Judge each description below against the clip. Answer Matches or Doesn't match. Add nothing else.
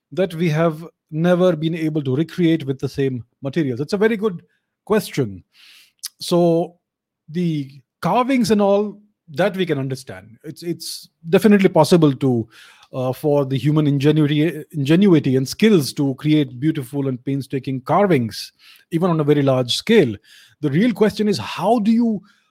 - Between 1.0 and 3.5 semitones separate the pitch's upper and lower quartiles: Doesn't match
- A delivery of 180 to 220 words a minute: Doesn't match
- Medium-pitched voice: Matches